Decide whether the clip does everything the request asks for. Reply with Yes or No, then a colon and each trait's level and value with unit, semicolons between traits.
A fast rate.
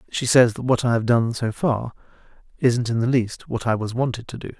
Yes: fast, 235 wpm